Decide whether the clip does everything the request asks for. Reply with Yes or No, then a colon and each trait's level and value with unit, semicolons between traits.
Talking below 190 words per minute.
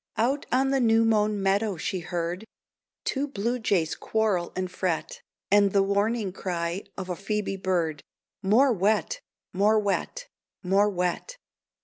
Yes: average, 140 wpm